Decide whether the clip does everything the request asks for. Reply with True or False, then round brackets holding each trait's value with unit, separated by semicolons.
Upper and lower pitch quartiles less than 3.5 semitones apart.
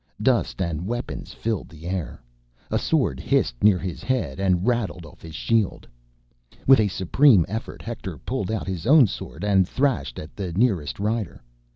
False (5.0 semitones)